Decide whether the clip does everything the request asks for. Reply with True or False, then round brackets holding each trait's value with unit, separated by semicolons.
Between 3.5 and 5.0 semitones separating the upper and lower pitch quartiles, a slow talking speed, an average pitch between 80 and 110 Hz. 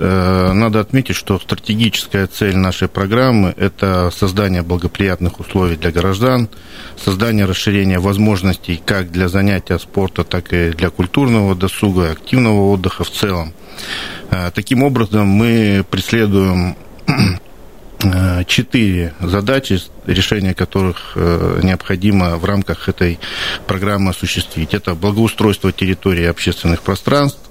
False (2.5 semitones; 105 wpm; 95 Hz)